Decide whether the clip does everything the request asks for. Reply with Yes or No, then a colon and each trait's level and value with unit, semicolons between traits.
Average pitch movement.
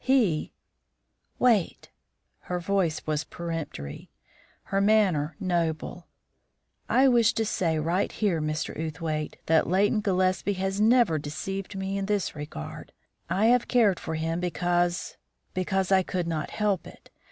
Yes: average, 3.8 semitones